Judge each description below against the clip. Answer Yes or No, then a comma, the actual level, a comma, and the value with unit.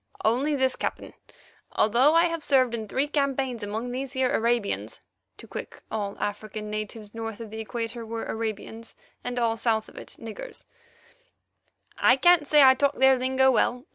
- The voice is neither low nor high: No, high, 240 Hz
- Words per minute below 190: Yes, average, 170 wpm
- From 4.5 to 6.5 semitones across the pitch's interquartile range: No, average, 3.2 semitones